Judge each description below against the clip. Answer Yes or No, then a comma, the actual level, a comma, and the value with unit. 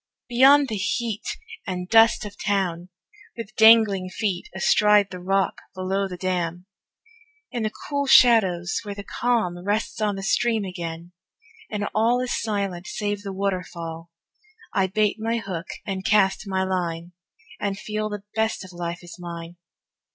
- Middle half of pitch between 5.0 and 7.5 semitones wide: No, average, 3.2 semitones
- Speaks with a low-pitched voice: No, high, 195 Hz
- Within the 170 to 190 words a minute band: No, average, 150 wpm